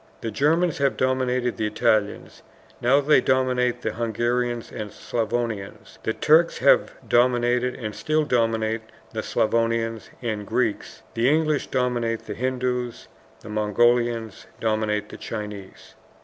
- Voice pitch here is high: No, low, 120 Hz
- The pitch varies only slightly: Yes, narrow, 2.3 semitones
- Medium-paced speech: No, slow, 125 wpm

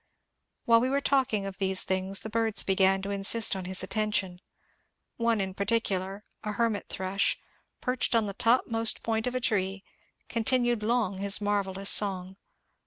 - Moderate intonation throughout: Yes, average, 3.0 semitones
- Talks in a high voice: Yes, high, 205 Hz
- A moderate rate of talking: Yes, average, 170 wpm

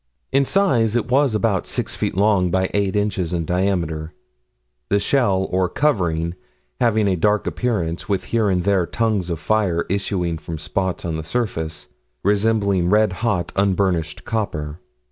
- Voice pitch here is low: Yes, very low, 95 Hz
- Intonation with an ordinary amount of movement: Yes, average, 3.9 semitones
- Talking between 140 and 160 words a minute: Yes, average, 155 wpm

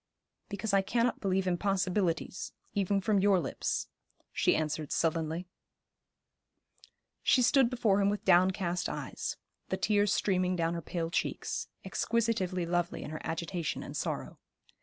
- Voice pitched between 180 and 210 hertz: Yes, medium, 185 Hz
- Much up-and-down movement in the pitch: No, average, 3.1 semitones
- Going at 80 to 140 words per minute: Yes, slow, 135 wpm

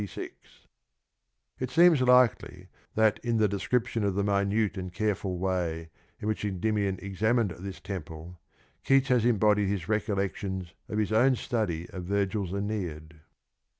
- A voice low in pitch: Yes, low, 100 Hz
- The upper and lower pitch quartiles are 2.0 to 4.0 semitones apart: Yes, average, 2.9 semitones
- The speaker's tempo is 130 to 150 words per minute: Yes, average, 140 wpm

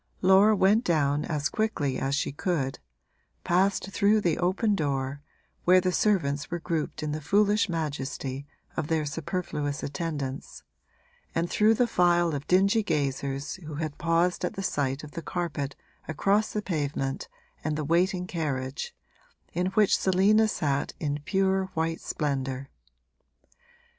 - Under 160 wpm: Yes, average, 145 wpm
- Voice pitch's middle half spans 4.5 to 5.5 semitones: Yes, average, 4.8 semitones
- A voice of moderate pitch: Yes, medium, 165 Hz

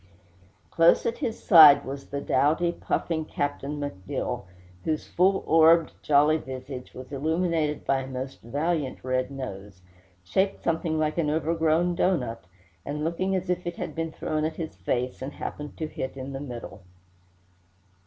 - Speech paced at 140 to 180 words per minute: Yes, average, 155 wpm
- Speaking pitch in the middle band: Yes, medium, 150 Hz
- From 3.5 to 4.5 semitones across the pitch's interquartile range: Yes, average, 3.8 semitones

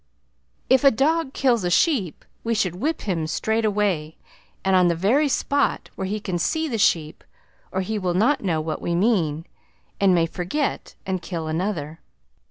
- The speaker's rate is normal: Yes, average, 180 wpm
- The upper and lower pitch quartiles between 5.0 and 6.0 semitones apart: Yes, wide, 5.5 semitones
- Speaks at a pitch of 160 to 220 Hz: Yes, high, 190 Hz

